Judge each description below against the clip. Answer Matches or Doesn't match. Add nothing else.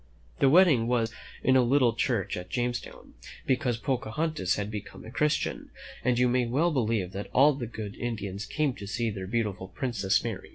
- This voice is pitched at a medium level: Doesn't match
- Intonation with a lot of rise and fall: Doesn't match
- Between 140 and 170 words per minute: Doesn't match